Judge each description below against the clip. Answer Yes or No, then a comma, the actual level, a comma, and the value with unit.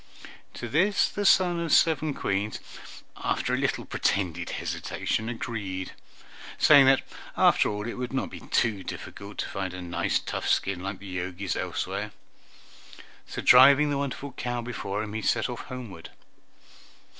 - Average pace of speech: Yes, average, 150 wpm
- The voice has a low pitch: Yes, low, 115 Hz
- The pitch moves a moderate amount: No, wide, 5.7 semitones